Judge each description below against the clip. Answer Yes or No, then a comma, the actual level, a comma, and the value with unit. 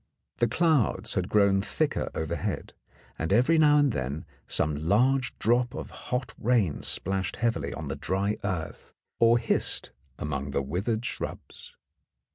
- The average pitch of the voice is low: Yes, low, 105 Hz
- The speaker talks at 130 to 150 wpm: Yes, average, 140 wpm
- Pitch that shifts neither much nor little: No, wide, 7.4 semitones